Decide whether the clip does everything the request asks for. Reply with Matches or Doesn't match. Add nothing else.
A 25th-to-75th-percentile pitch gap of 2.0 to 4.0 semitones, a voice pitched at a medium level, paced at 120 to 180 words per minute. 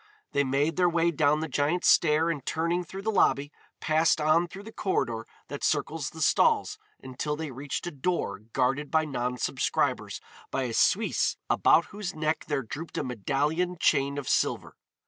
Matches